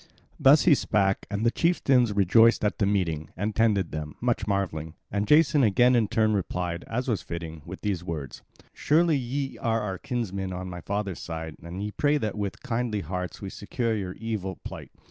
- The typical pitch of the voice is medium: No, low, 105 Hz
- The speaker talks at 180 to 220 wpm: Yes, average, 190 wpm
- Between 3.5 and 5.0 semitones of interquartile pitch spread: Yes, average, 4.3 semitones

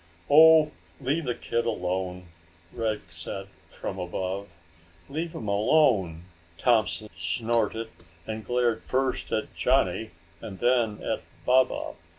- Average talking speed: No, slow, 115 wpm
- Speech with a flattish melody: No, average, 4.7 semitones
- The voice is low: Yes, low, 110 Hz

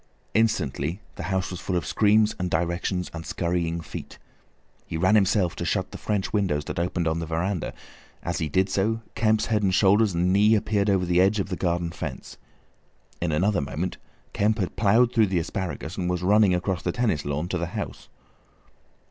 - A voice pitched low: Yes, very low, 95 Hz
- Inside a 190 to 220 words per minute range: Yes, average, 195 wpm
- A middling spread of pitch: Yes, average, 3.3 semitones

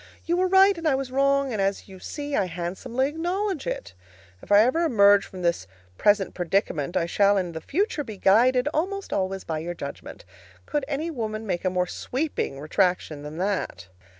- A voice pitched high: Yes, high, 205 Hz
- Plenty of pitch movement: Yes, wide, 8.0 semitones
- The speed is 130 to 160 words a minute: No, average, 190 wpm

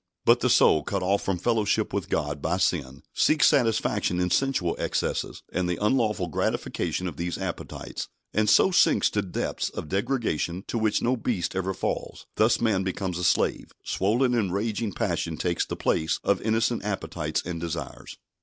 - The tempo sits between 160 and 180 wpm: Yes, average, 175 wpm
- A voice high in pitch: No, very low, 95 Hz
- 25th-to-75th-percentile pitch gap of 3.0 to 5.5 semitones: Yes, average, 4.3 semitones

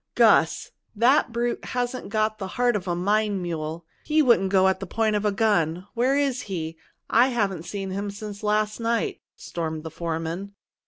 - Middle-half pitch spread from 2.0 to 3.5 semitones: No, average, 4.4 semitones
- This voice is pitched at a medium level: No, high, 205 Hz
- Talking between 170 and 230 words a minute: Yes, average, 180 wpm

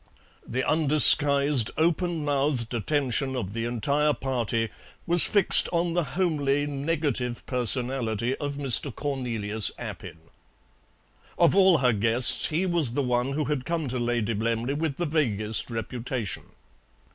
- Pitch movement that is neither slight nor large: Yes, average, 4.2 semitones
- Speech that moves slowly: Yes, slow, 130 wpm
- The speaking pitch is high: No, low, 135 Hz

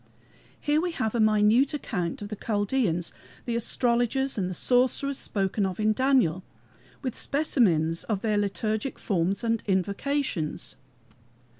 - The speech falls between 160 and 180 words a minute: No, slow, 135 wpm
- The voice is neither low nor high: No, high, 215 Hz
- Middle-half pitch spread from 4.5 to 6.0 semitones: Yes, average, 5.0 semitones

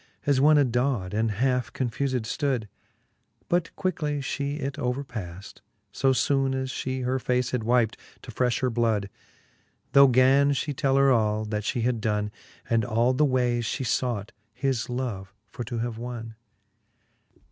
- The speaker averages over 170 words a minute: No, average, 160 wpm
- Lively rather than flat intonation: No, average, 3.1 semitones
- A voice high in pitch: No, low, 125 Hz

